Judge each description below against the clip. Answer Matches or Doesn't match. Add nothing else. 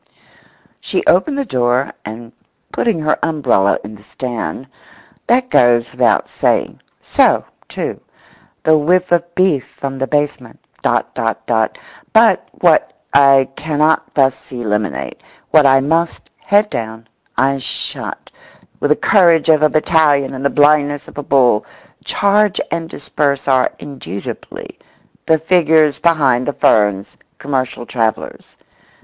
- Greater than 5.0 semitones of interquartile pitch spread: Doesn't match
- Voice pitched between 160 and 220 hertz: Doesn't match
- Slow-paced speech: Matches